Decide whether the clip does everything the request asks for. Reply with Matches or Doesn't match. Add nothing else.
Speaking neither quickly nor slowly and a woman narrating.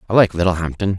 Doesn't match